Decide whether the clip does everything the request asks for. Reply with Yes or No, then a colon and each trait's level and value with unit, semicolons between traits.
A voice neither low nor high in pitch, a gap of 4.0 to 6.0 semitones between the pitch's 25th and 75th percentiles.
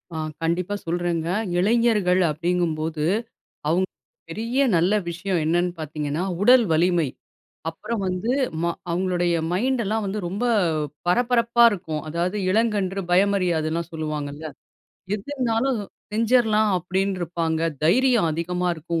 Yes: medium, 180 Hz; average, 4.3 semitones